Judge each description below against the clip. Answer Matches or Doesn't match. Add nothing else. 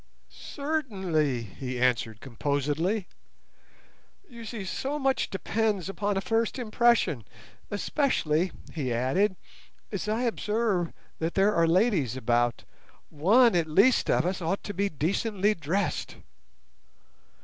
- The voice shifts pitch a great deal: Matches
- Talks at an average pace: Doesn't match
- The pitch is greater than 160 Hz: Matches